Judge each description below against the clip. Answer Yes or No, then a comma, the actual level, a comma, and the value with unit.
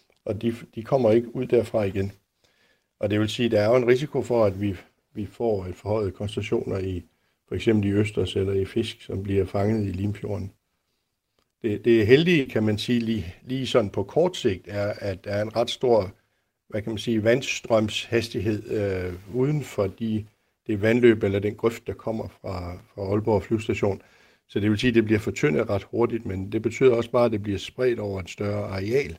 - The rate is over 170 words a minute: Yes, average, 205 wpm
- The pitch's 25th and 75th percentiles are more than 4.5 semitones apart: No, average, 2.7 semitones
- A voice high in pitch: No, low, 105 Hz